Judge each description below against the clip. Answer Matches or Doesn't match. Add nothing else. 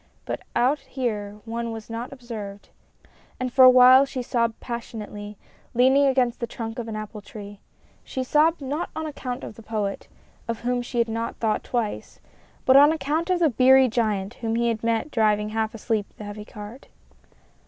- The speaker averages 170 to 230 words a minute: Matches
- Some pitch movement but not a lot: Matches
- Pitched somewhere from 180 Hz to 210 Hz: Doesn't match